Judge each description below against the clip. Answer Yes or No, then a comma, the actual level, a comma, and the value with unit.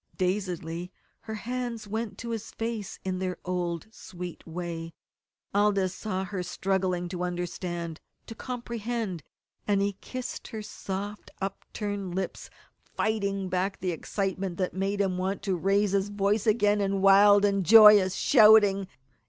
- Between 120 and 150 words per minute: Yes, average, 140 wpm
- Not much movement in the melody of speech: Yes, narrow, 2.3 semitones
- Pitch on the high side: Yes, high, 195 Hz